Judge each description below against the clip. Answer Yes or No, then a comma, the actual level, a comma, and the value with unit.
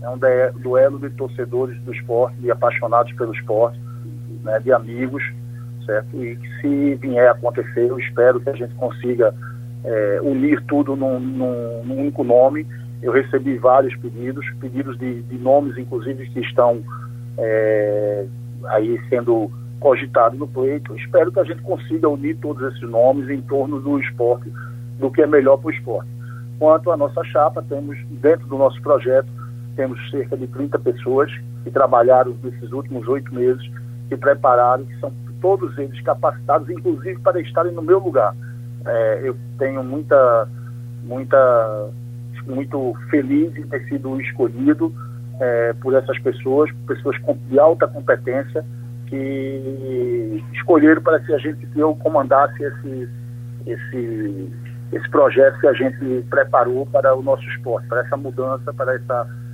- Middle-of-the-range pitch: No, low, 125 Hz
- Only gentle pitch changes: Yes, narrow, 2.1 semitones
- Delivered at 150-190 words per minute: Yes, average, 155 wpm